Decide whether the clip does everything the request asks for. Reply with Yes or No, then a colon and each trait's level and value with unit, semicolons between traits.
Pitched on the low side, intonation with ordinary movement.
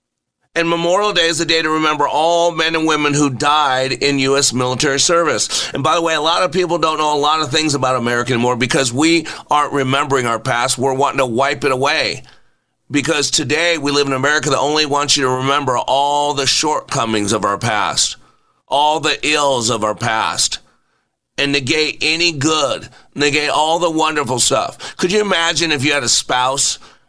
No: medium, 145 Hz; average, 3.2 semitones